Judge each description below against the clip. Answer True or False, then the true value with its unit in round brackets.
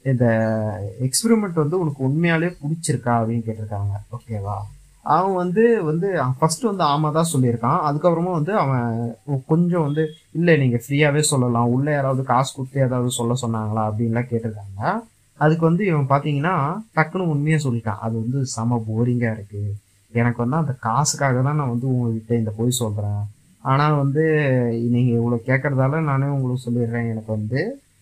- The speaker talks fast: True (145 wpm)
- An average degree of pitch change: True (4.6 semitones)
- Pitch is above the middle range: False (130 Hz)